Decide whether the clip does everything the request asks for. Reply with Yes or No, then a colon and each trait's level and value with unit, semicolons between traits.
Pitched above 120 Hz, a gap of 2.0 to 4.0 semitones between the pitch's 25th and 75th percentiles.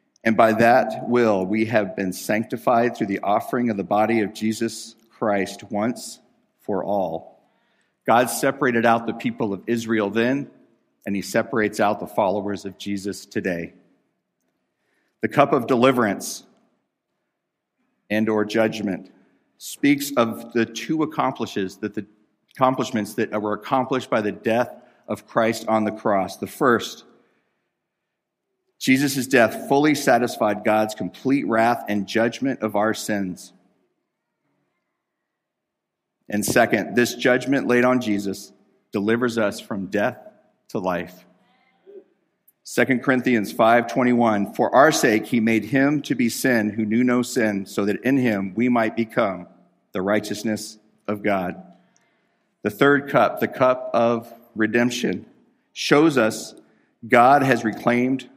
No: low, 115 Hz; average, 2.9 semitones